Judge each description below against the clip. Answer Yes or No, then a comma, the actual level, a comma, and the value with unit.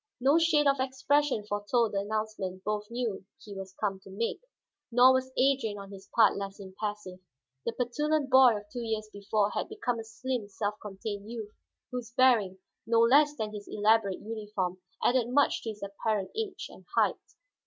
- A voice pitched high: Yes, high, 220 Hz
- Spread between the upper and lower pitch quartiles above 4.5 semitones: No, average, 3.8 semitones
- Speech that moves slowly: No, average, 175 wpm